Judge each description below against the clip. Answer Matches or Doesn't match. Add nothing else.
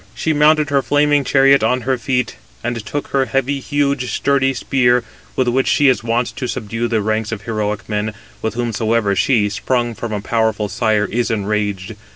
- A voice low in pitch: Matches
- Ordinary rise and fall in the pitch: Matches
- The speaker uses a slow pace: Doesn't match